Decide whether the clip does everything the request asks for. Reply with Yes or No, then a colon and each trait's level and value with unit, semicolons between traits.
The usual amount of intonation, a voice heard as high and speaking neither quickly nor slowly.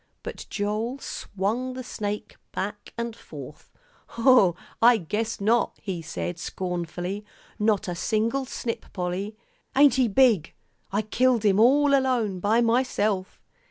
No: average, 3.9 semitones; high, 215 Hz; slow, 130 wpm